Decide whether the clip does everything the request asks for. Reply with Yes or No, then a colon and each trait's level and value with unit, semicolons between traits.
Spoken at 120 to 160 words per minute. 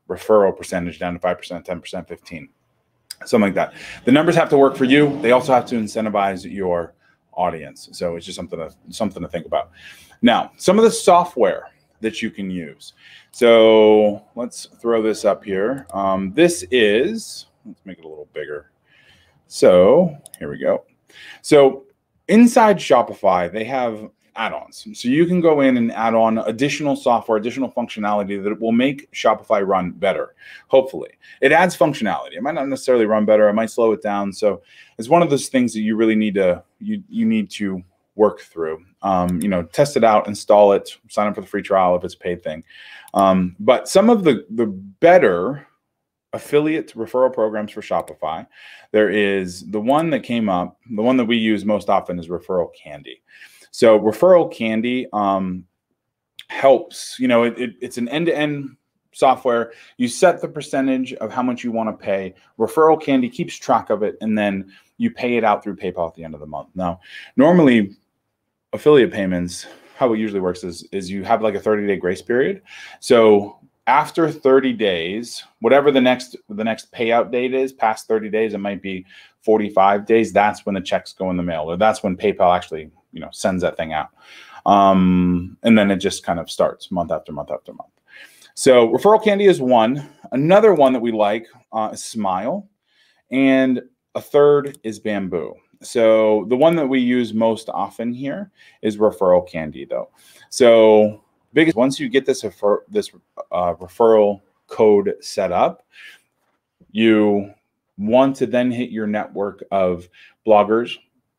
No: average, 180 wpm